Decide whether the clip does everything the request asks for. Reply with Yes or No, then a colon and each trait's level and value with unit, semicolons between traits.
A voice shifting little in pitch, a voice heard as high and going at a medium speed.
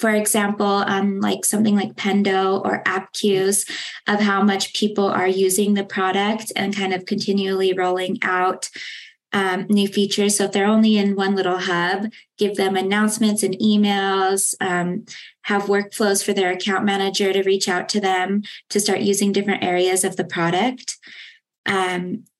Yes: narrow, 1.3 semitones; high, 195 Hz; average, 165 wpm